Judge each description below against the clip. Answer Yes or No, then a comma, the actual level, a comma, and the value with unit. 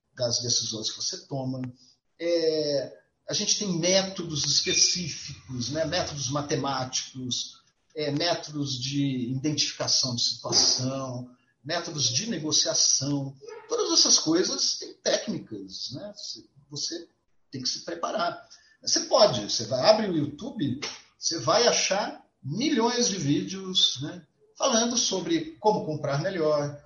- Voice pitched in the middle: Yes, medium, 155 Hz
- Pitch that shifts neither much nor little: No, wide, 6.3 semitones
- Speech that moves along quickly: No, slow, 120 wpm